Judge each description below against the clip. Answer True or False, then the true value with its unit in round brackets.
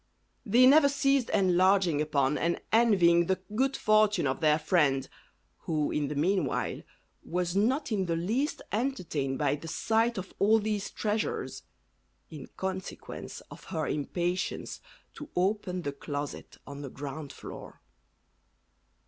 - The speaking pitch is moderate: True (180 Hz)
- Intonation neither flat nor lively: False (6.0 semitones)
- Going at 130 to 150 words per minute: True (135 wpm)